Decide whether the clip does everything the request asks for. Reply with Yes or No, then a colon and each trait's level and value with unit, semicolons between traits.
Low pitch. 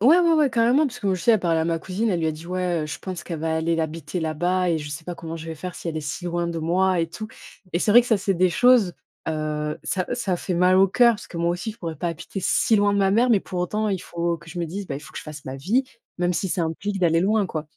No: medium, 175 Hz